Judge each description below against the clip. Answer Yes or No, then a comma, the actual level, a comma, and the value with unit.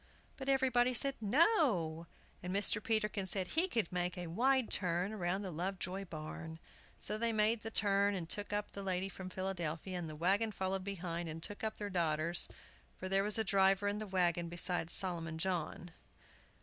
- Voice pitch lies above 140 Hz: Yes, high, 190 Hz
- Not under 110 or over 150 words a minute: No, average, 185 wpm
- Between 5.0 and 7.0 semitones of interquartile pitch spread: No, average, 3.4 semitones